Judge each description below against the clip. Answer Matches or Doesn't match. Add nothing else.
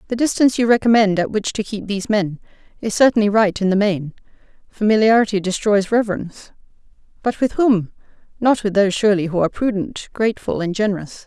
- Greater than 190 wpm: Doesn't match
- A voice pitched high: Matches